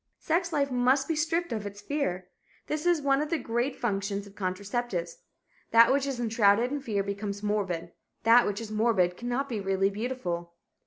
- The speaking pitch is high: Yes, high, 225 Hz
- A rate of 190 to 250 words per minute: No, average, 180 wpm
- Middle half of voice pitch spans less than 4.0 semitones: No, average, 5.3 semitones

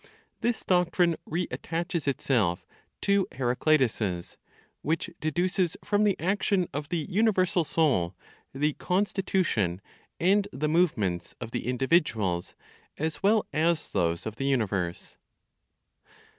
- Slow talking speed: Yes, slow, 110 wpm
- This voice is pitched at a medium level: Yes, medium, 155 Hz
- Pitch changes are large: Yes, wide, 7.6 semitones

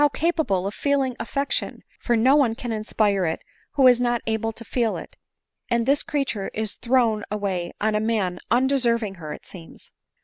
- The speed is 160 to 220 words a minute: Yes, average, 175 wpm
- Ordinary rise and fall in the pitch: Yes, average, 3.7 semitones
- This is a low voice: No, high, 230 Hz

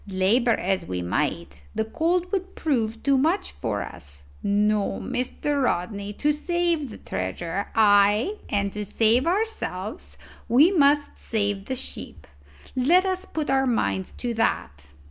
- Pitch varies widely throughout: Yes, wide, 7.1 semitones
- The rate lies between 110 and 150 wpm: Yes, average, 145 wpm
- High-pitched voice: Yes, high, 225 Hz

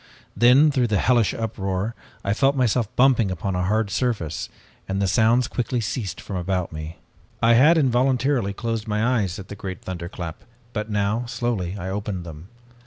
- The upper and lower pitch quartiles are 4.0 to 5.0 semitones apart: Yes, average, 4.3 semitones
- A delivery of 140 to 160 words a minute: No, average, 175 wpm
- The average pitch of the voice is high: No, low, 105 Hz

